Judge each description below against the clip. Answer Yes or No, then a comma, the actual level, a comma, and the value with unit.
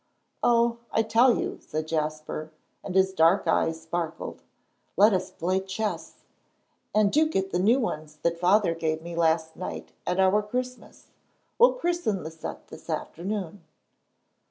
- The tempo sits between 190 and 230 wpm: No, average, 150 wpm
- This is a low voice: No, medium, 185 Hz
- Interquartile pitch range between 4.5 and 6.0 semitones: Yes, average, 4.8 semitones